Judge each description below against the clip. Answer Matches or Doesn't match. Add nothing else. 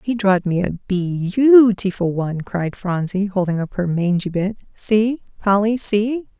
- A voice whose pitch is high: Matches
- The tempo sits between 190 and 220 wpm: Doesn't match